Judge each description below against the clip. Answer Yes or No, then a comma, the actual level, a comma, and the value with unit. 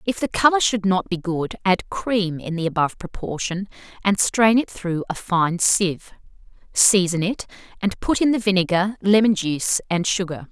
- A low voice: No, high, 190 Hz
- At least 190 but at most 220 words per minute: No, average, 175 wpm